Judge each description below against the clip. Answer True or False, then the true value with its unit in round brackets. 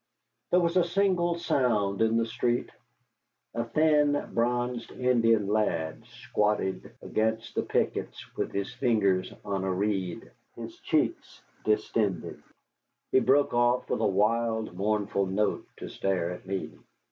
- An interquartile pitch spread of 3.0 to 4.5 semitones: True (3.9 semitones)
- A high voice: False (110 Hz)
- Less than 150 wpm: True (135 wpm)